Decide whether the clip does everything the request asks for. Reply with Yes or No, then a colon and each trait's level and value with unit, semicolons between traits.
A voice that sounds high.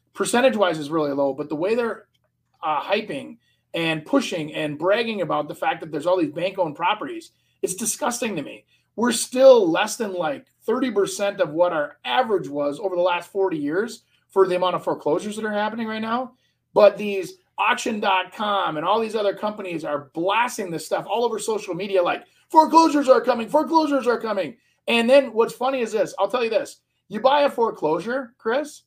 Yes: high, 220 Hz